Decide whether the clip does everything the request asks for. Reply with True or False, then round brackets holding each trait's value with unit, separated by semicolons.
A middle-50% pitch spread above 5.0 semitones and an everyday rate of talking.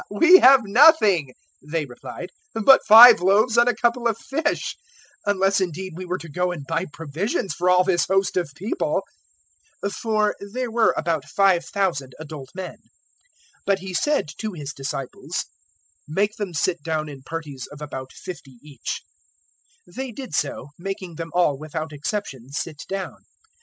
True (5.4 semitones; 160 wpm)